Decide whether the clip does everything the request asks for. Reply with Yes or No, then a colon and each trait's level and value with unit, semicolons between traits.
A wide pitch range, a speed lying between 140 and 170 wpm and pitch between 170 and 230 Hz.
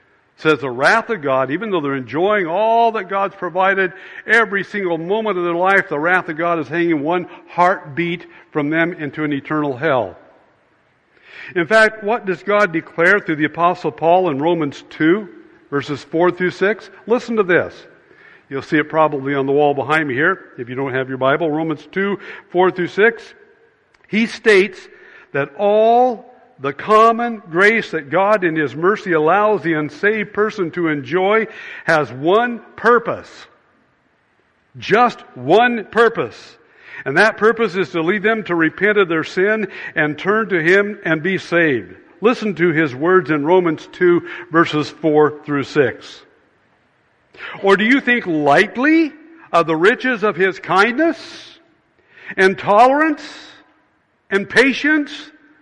Yes: wide, 5.8 semitones; average, 155 wpm; medium, 185 Hz